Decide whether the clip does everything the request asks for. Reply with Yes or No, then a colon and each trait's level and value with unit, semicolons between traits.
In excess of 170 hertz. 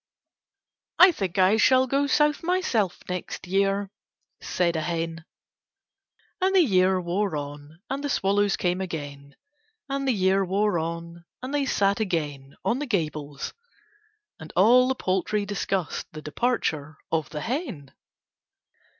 Yes: high, 190 Hz